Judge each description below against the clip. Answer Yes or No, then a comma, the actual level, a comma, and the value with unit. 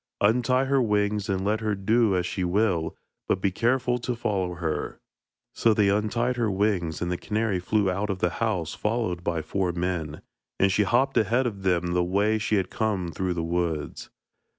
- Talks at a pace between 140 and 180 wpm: No, average, 195 wpm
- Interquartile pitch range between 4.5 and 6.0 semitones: No, average, 3.7 semitones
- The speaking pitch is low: Yes, low, 100 Hz